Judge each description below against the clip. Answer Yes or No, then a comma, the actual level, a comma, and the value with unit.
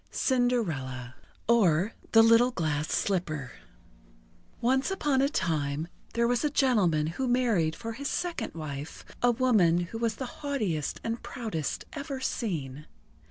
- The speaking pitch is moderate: No, high, 225 Hz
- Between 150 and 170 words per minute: No, average, 140 wpm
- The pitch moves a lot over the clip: Yes, wide, 8.0 semitones